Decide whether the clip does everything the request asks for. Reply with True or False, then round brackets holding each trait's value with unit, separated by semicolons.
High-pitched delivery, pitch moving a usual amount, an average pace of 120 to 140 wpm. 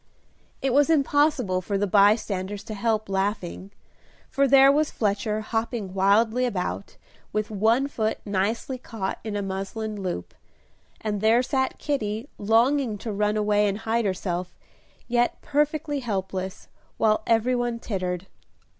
True (215 Hz; 3.5 semitones; 135 wpm)